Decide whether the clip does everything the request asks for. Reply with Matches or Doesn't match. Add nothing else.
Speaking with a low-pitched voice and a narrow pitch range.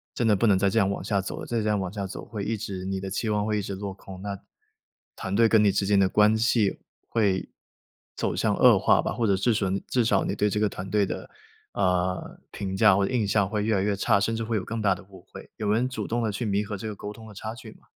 Matches